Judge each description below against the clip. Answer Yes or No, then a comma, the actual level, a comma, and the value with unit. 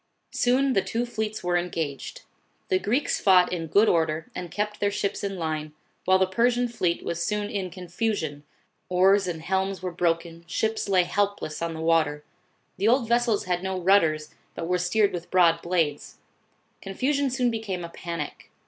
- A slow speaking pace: No, average, 175 wpm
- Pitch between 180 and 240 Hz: Yes, medium, 185 Hz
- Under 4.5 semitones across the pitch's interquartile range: Yes, average, 3.9 semitones